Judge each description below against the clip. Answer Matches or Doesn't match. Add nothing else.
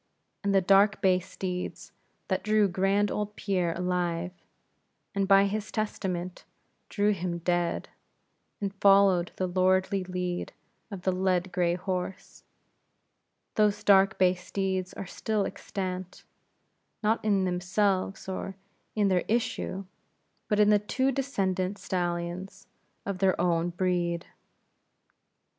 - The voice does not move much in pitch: Matches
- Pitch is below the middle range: Doesn't match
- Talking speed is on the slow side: Matches